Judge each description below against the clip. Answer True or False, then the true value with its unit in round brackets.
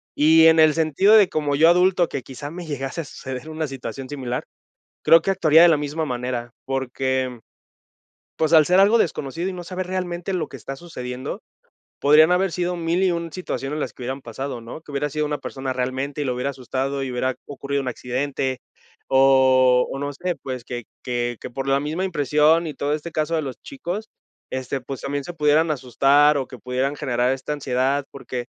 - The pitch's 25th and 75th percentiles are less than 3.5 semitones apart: False (3.8 semitones)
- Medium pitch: True (145 Hz)